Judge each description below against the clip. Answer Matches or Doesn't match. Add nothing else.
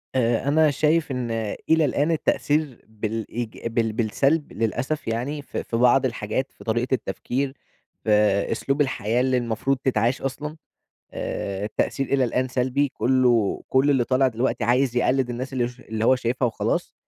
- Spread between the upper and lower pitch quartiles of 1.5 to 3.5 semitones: Matches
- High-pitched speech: Doesn't match